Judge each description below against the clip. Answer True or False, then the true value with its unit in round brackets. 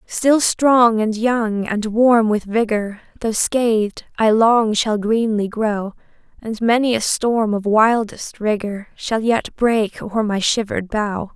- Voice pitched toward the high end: True (220 Hz)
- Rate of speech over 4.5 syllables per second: False (3.7 syllables/s)